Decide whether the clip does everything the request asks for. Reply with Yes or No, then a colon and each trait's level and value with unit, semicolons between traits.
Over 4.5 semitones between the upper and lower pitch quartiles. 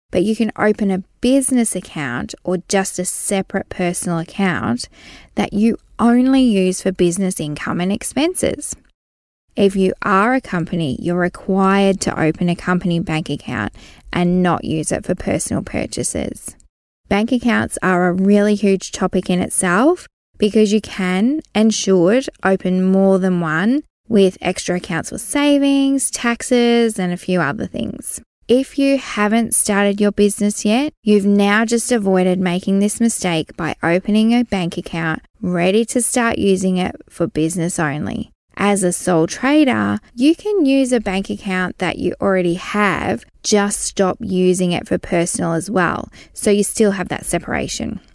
No: average, 4.0 semitones